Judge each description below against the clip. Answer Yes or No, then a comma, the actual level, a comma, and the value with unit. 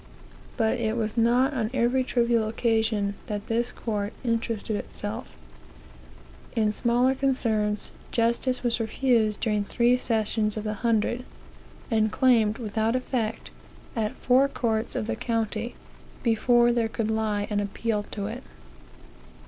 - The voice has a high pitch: Yes, high, 225 Hz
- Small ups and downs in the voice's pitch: Yes, narrow, 1.9 semitones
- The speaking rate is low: Yes, slow, 130 wpm